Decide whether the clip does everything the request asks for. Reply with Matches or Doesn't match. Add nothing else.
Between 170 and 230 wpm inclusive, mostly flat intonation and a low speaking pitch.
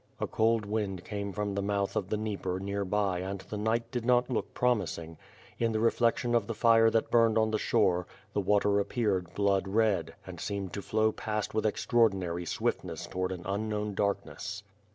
Matches